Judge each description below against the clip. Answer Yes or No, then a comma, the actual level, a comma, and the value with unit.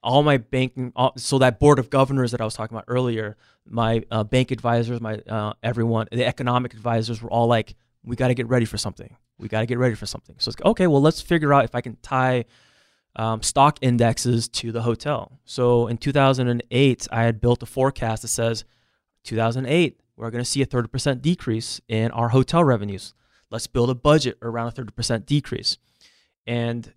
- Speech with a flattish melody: Yes, narrow, 2.2 semitones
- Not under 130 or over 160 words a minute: No, average, 200 wpm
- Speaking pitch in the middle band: No, low, 120 Hz